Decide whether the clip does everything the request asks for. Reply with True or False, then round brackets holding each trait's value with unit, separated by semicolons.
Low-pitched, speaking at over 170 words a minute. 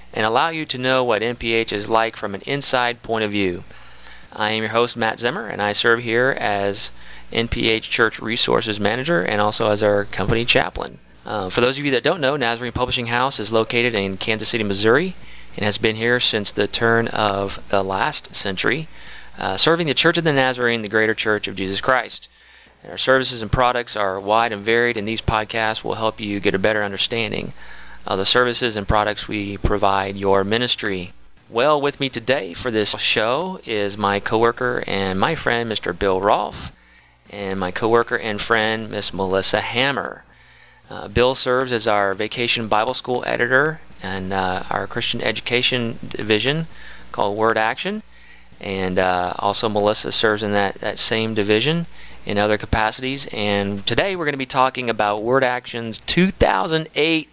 True (110 Hz; 180 wpm)